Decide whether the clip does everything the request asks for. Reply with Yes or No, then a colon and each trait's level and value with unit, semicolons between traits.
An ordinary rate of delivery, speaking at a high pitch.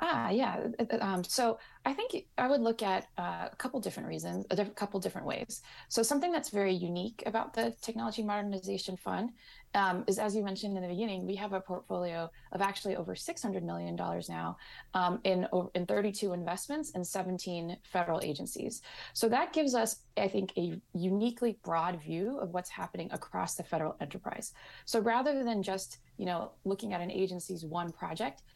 Yes: average, 185 wpm; high, 195 Hz